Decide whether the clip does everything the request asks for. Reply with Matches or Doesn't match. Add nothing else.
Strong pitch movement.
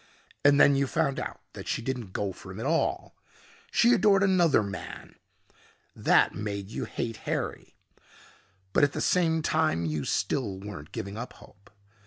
Matches